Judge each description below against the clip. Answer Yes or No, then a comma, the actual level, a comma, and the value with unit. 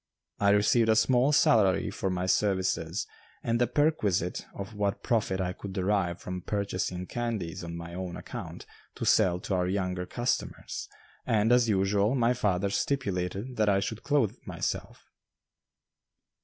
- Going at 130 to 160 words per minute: Yes, average, 150 wpm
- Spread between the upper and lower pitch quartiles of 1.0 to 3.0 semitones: No, average, 3.8 semitones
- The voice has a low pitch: Yes, low, 100 Hz